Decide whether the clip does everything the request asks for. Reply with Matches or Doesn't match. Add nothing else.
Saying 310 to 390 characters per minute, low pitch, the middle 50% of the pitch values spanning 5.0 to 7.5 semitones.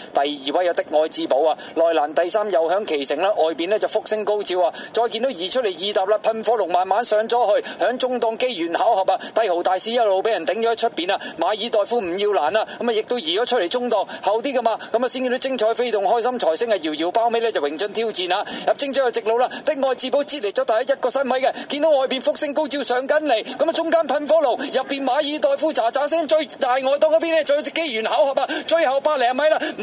Doesn't match